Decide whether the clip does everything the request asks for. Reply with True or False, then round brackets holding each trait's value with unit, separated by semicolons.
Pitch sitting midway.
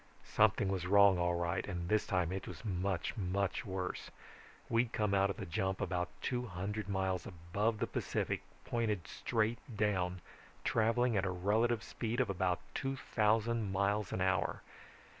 False (100 Hz)